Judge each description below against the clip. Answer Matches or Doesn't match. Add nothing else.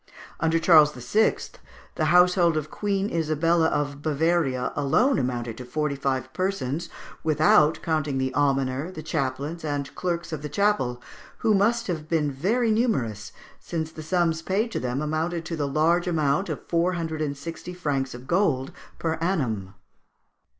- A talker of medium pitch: Matches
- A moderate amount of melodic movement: Matches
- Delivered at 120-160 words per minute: Matches